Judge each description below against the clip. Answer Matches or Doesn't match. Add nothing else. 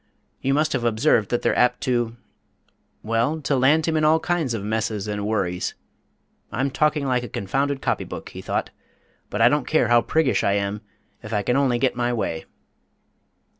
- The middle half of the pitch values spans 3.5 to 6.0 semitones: Matches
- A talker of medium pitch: Doesn't match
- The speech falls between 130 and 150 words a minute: Doesn't match